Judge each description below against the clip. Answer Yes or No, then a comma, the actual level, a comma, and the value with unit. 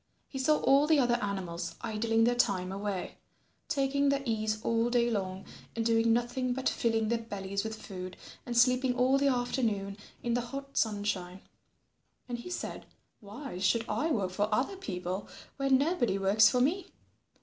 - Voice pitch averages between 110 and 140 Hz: No, high, 230 Hz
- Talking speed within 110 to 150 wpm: No, average, 170 wpm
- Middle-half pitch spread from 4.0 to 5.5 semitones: Yes, average, 4.4 semitones